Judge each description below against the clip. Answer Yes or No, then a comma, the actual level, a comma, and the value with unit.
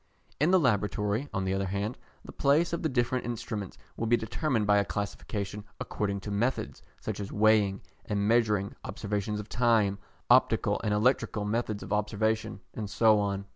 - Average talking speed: Yes, average, 175 wpm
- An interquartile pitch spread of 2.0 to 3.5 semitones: Yes, narrow, 2.4 semitones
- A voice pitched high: No, low, 105 Hz